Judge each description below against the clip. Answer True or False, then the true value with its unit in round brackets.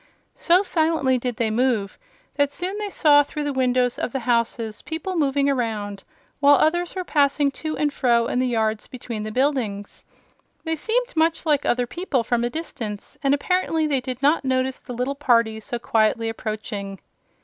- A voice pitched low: False (260 Hz)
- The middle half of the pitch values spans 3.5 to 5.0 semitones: True (4.5 semitones)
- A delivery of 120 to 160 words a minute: False (180 wpm)